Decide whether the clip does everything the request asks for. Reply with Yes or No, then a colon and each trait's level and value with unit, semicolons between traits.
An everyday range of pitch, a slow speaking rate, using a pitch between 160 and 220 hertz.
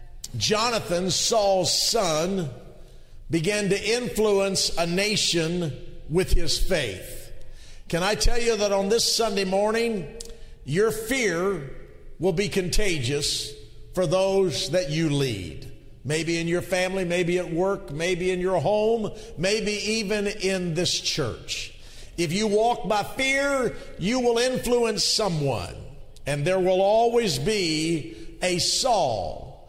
Yes: average, 4.6 semitones; slow, 125 wpm; medium, 185 Hz